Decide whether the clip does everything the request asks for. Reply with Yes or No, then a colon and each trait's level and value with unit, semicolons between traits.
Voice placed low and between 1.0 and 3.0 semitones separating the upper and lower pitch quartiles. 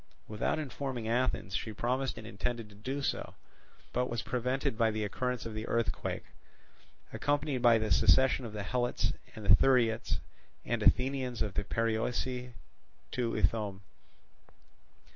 Yes: low, 120 Hz; narrow, 2.6 semitones